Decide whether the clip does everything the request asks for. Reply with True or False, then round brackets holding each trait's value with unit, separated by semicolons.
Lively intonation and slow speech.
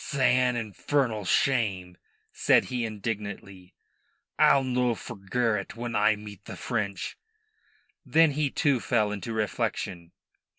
False (3.8 semitones; 115 wpm)